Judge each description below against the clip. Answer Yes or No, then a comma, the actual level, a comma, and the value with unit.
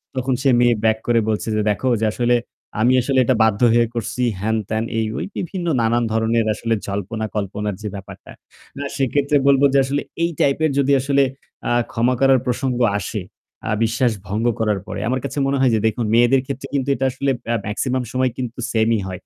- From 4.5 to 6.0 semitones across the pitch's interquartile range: No, average, 3.3 semitones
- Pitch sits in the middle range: No, low, 120 Hz